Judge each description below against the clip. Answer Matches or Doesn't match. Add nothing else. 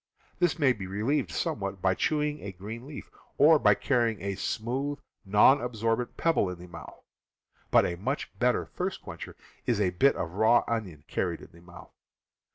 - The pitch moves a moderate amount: Doesn't match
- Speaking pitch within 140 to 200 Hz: Doesn't match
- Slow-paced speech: Doesn't match